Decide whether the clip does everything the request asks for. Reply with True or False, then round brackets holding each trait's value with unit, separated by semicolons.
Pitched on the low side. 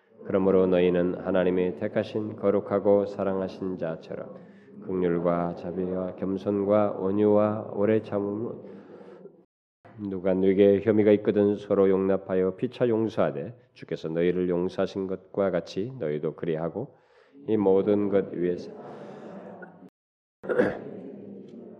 True (95 Hz)